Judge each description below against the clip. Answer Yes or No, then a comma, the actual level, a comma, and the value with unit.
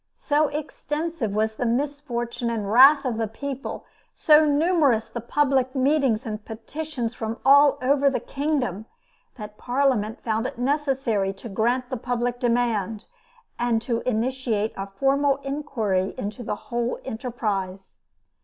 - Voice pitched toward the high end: Yes, high, 245 Hz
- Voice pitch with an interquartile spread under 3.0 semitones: No, average, 4.1 semitones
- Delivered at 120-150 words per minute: Yes, average, 140 wpm